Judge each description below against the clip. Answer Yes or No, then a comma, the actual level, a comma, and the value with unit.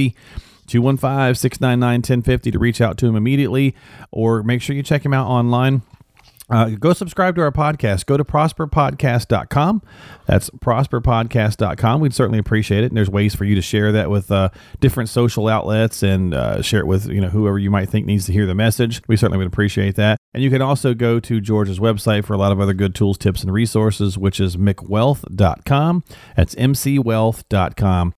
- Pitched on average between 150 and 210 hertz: No, low, 115 Hz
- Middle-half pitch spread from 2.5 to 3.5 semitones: No, average, 4.2 semitones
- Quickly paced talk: No, average, 190 wpm